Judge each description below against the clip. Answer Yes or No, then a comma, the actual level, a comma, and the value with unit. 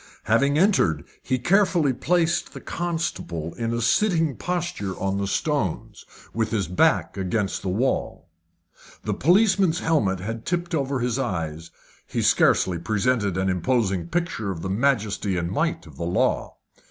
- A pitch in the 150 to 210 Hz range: No, low, 115 Hz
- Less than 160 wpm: Yes, average, 150 wpm